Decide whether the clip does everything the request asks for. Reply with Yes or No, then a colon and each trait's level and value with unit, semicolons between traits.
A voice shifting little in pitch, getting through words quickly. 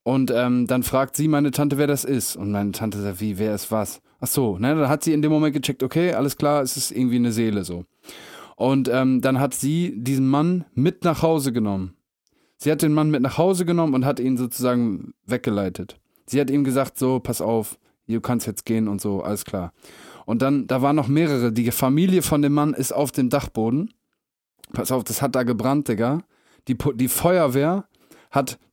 No: average, 3.5 semitones; fast, 215 wpm